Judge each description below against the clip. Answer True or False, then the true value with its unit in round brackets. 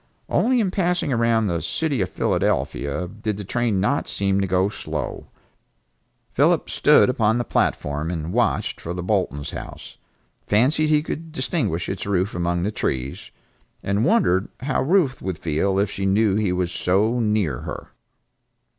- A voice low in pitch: True (100 Hz)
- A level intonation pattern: False (5.3 semitones)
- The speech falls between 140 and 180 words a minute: True (160 wpm)